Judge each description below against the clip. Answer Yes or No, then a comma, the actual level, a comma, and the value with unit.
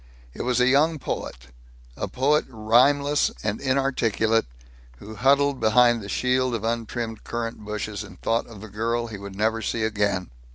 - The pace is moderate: Yes, average, 165 wpm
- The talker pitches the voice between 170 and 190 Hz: No, low, 115 Hz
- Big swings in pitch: No, average, 3.2 semitones